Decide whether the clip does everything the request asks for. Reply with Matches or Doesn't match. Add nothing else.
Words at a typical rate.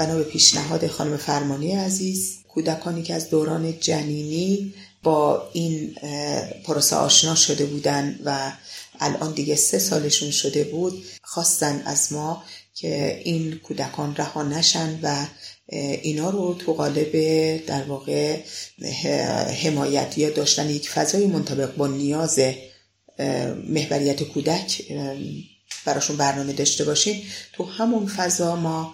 Matches